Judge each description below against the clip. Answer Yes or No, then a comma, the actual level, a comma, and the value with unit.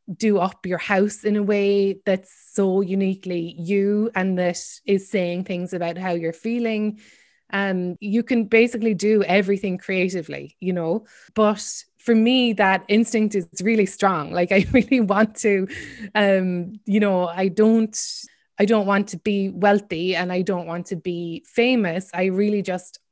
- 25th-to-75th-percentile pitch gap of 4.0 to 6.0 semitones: No, narrow, 2.6 semitones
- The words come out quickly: No, average, 165 wpm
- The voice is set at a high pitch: Yes, high, 195 Hz